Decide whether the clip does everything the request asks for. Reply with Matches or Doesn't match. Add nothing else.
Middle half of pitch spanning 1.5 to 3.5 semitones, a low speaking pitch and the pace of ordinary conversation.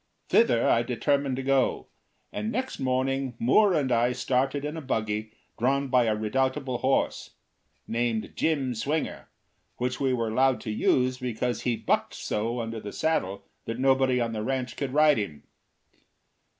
Matches